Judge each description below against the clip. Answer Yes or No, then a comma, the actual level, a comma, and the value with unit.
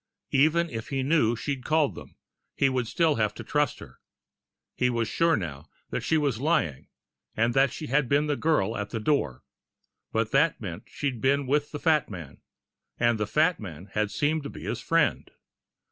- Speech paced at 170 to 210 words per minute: Yes, average, 190 wpm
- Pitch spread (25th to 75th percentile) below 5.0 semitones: No, average, 5.3 semitones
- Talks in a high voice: No, low, 135 Hz